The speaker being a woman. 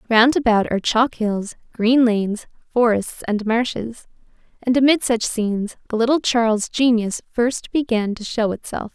Yes: female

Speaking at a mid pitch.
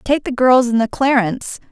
No: high, 245 Hz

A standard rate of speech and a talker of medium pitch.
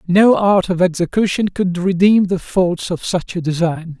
Yes: average, 180 wpm; medium, 180 Hz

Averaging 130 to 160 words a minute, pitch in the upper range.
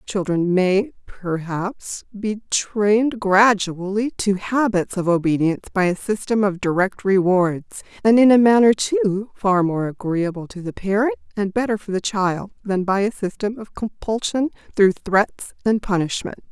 Yes: average, 155 wpm; high, 200 Hz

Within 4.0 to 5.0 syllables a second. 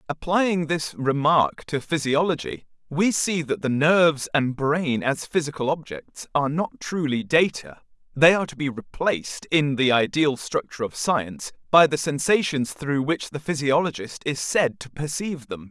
Yes: 4.7 syllables/s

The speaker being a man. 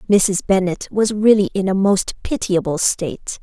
No: female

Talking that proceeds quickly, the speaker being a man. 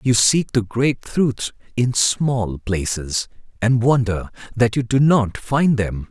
No: average, 155 wpm; male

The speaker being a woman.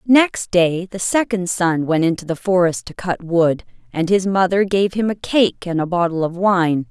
Yes: female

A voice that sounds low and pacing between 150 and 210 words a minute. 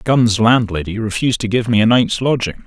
Yes: low, 110 Hz; average, 200 wpm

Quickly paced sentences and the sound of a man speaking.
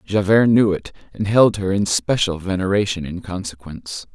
No: average, 160 wpm; male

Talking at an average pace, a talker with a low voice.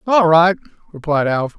No: average, 150 wpm; medium, 165 Hz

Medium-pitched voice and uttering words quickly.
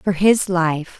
No: medium, 180 Hz; average, 180 wpm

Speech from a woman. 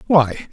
No: male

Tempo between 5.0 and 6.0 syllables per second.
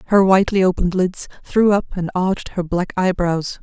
Yes: 5.5 syllables/s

